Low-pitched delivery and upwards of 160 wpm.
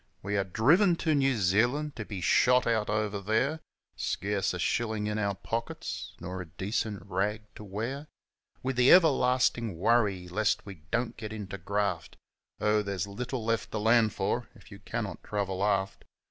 Yes: low, 105 Hz; average, 170 wpm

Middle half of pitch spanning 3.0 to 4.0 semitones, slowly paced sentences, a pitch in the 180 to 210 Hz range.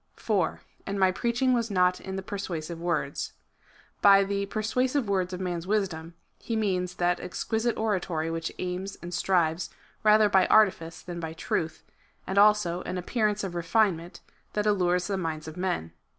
No: average, 3.4 semitones; average, 165 wpm; medium, 185 Hz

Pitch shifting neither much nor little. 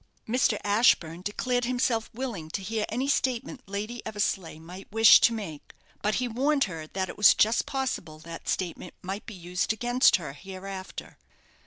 Yes: average, 4.8 semitones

